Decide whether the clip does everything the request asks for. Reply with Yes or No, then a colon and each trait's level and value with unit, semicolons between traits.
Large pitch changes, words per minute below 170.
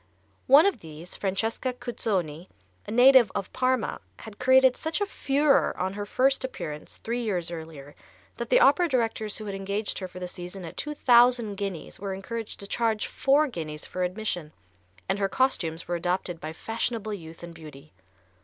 No: wide, 6.0 semitones; average, 175 wpm